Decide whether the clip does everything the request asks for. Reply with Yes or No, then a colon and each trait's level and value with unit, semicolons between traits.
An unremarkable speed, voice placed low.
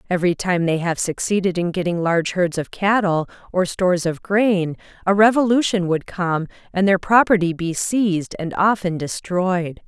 No: average, 165 wpm; medium, 185 Hz